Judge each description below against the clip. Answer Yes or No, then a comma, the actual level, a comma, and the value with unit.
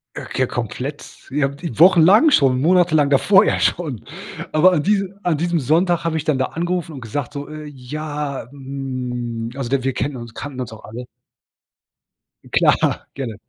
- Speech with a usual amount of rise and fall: Yes, average, 4.5 semitones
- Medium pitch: Yes, medium, 145 Hz